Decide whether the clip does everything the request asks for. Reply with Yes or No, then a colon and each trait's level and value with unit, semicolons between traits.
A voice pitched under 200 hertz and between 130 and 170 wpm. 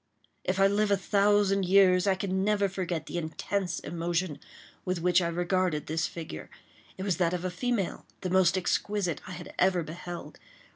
No: medium, 185 Hz; average, 180 wpm